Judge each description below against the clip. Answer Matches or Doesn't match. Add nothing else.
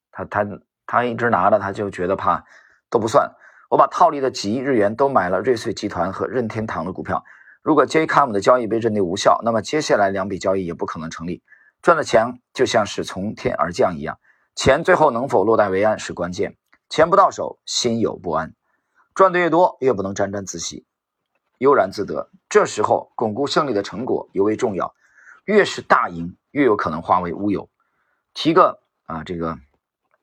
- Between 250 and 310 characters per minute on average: Matches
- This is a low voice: Matches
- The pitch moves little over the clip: Doesn't match